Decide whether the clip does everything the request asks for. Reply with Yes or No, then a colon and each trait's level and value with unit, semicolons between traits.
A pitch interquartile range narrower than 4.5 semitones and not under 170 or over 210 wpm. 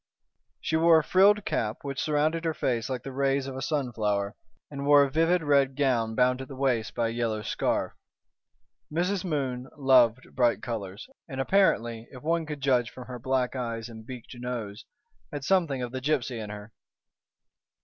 Yes: average, 3.8 semitones; average, 180 wpm